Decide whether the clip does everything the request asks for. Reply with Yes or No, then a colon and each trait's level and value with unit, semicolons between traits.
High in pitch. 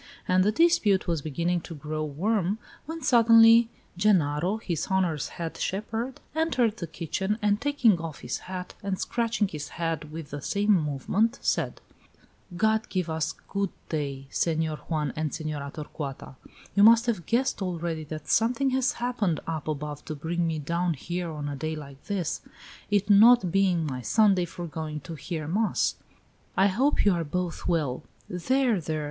No: medium, 175 Hz